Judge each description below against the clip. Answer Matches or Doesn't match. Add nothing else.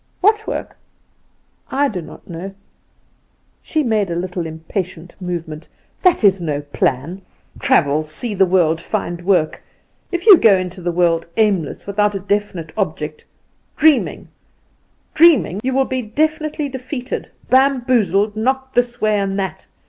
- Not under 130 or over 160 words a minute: Matches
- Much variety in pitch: Matches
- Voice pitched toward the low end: Doesn't match